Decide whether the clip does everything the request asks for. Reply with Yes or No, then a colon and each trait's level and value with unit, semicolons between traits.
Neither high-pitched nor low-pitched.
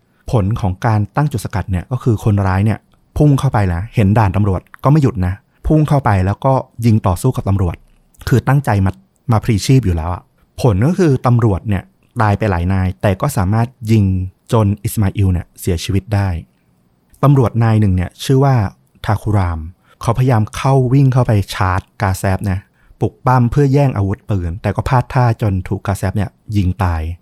No: low, 105 Hz